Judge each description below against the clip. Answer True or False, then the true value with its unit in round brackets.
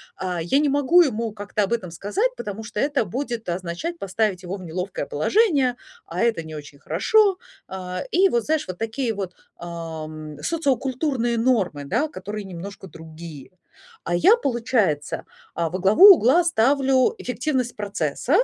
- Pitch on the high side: True (215 Hz)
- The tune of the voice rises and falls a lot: True (7.4 semitones)